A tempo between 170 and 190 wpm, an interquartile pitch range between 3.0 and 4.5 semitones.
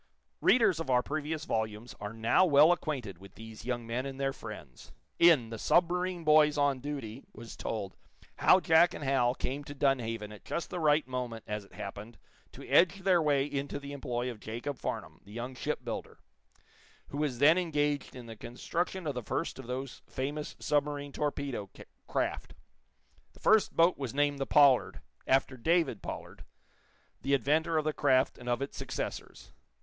Yes: average, 175 wpm; average, 4.1 semitones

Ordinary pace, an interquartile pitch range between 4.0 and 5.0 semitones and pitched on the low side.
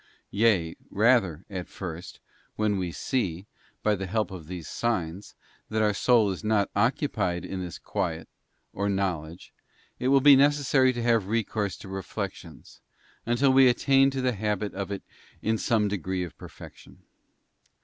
Yes: average, 155 wpm; average, 4.4 semitones; low, 105 Hz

